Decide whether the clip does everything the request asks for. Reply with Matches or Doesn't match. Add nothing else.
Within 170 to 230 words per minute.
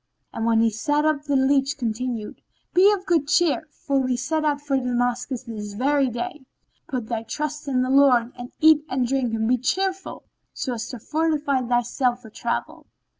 Matches